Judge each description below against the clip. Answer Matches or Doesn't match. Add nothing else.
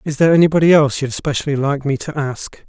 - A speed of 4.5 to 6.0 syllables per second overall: Doesn't match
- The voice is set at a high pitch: Doesn't match